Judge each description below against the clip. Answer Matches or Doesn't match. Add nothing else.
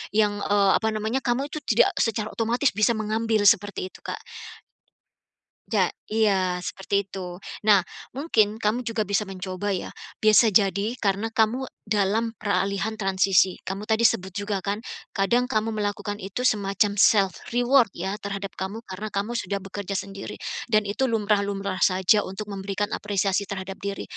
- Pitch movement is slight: Matches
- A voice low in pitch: Doesn't match